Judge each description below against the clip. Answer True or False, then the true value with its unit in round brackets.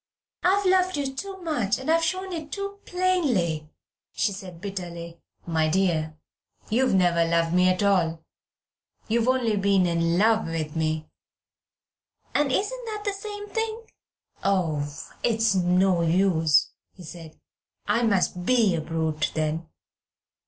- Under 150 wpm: True (140 wpm)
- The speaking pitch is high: True (195 Hz)